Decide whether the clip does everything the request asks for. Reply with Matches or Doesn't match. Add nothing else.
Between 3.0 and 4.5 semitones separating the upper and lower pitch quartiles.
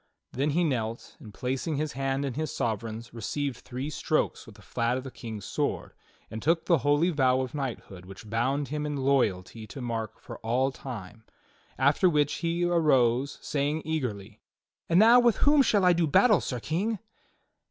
Doesn't match